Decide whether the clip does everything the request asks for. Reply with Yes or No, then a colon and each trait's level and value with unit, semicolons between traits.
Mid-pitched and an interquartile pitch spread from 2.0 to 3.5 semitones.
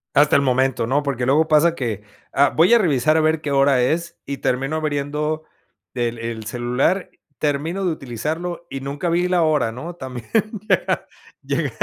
No: medium, 145 Hz; average, 3.9 semitones